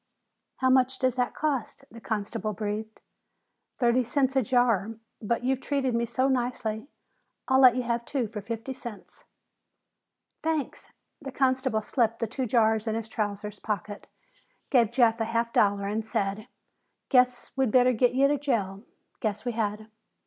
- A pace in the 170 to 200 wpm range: No, average, 155 wpm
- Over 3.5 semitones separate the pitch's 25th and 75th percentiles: No, average, 3.1 semitones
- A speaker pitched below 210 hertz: No, high, 235 Hz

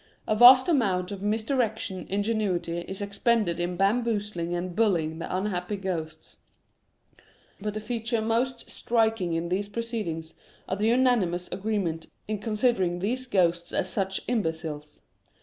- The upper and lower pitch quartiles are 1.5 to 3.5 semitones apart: No, average, 4.4 semitones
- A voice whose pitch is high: Yes, high, 200 Hz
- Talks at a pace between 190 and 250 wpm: No, average, 140 wpm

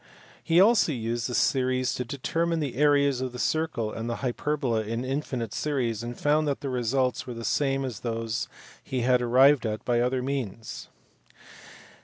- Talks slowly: No, average, 175 wpm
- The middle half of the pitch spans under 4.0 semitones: Yes, average, 3.2 semitones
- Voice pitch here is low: Yes, low, 130 Hz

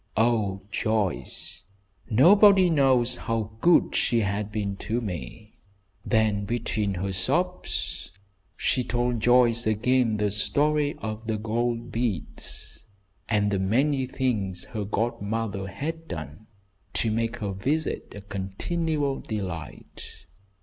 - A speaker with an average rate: No, slow, 115 wpm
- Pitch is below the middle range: Yes, low, 110 Hz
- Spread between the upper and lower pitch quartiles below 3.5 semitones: No, average, 3.8 semitones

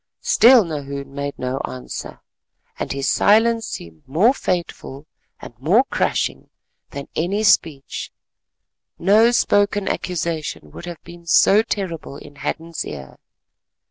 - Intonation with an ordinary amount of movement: No, wide, 6.6 semitones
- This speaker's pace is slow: Yes, slow, 120 wpm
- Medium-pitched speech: Yes, medium, 165 Hz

